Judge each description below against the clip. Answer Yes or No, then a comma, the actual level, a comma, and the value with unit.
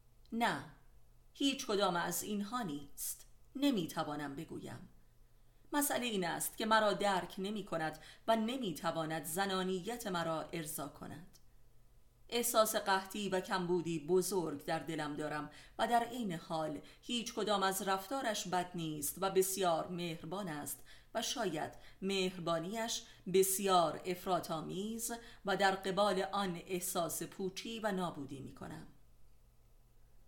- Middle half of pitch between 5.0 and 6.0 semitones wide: No, average, 4.0 semitones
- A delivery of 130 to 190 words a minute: No, average, 120 wpm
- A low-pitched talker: No, medium, 185 Hz